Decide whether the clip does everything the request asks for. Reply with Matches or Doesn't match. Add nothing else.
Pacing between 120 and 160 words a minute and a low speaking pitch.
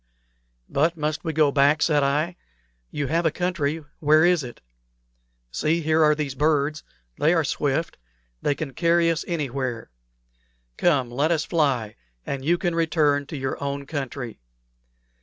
Doesn't match